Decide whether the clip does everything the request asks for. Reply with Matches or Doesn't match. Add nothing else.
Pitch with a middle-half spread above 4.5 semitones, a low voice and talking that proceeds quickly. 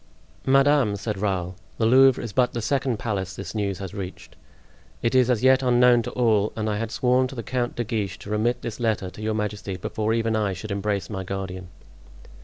Doesn't match